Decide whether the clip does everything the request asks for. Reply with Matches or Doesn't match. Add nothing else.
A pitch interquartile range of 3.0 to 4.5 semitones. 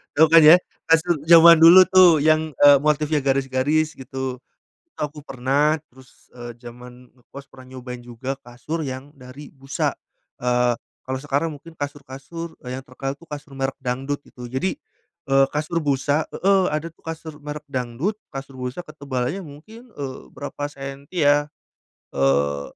Matches